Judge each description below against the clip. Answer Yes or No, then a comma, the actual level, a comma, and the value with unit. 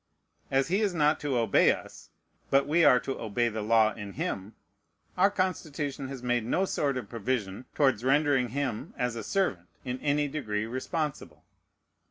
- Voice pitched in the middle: No, low, 130 Hz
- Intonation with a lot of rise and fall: No, average, 4.7 semitones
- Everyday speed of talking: Yes, average, 170 wpm